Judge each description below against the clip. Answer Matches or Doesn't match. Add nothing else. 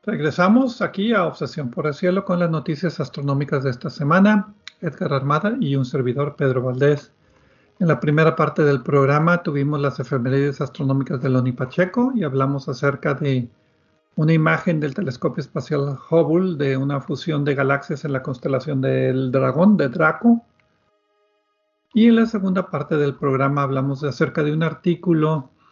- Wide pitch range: Doesn't match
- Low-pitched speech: Doesn't match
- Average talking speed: Matches